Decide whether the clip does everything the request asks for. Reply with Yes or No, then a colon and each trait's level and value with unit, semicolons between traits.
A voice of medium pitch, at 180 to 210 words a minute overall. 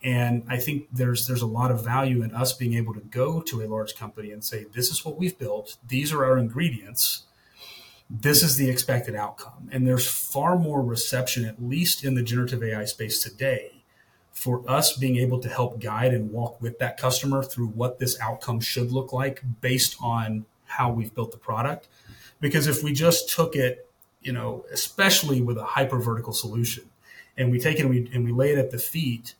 No: low, 125 Hz; fast, 205 wpm